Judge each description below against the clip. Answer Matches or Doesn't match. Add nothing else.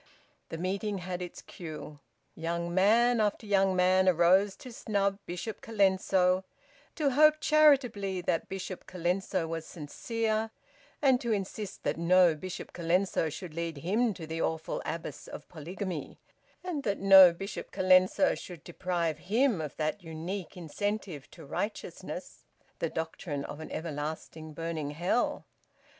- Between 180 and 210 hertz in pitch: Matches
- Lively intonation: Doesn't match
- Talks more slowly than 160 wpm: Matches